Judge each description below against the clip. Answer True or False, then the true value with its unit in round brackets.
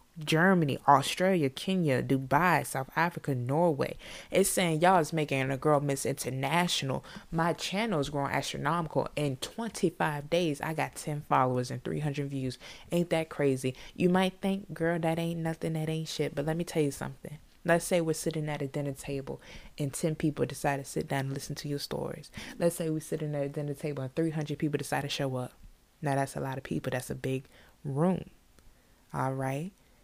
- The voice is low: False (150 Hz)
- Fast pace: False (195 wpm)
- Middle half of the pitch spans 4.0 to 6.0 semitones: False (3.2 semitones)